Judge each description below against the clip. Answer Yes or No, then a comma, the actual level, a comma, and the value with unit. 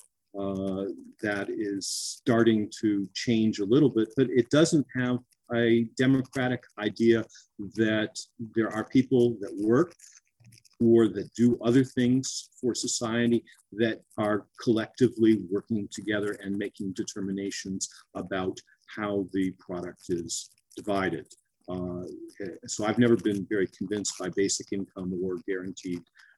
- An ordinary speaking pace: No, slow, 125 wpm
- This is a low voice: Yes, low, 110 Hz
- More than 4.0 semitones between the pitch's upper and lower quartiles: No, average, 3.3 semitones